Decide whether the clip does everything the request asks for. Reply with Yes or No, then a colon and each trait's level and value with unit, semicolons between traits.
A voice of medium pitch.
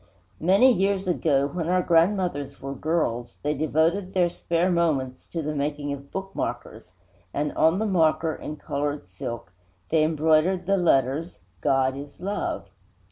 Yes: medium, 160 Hz